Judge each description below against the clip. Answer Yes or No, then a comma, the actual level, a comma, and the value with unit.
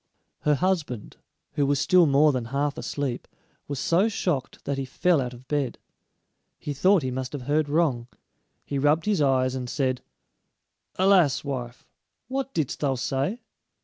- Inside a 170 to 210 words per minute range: No, average, 160 wpm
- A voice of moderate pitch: Yes, medium, 145 Hz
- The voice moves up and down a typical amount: Yes, average, 3.8 semitones